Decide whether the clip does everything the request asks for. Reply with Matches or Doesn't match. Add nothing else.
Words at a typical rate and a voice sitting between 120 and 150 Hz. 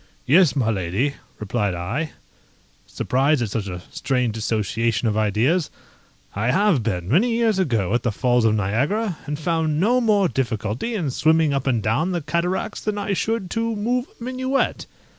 Matches